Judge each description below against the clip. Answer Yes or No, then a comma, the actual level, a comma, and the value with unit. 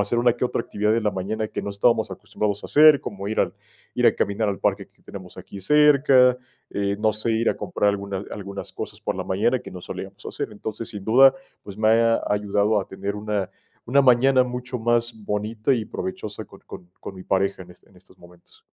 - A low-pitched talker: Yes, low, 105 Hz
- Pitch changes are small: No, average, 3.1 semitones